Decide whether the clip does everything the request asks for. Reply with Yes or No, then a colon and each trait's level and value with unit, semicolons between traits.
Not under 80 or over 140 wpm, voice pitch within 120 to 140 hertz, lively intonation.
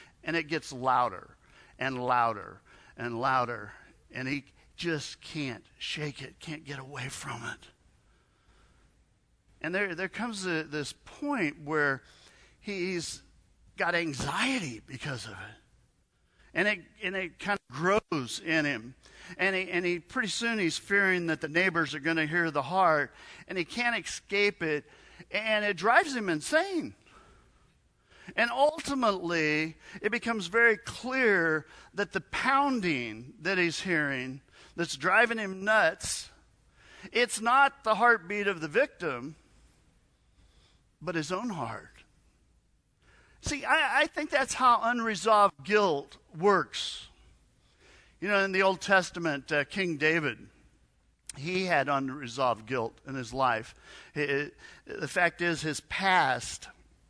No: slow, 135 wpm; medium, 170 Hz; wide, 6.5 semitones